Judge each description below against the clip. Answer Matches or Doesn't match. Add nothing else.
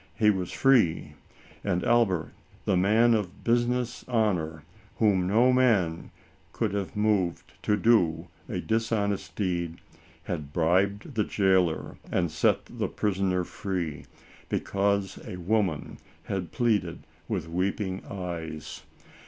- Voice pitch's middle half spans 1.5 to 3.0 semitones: Doesn't match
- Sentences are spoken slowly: Matches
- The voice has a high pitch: Doesn't match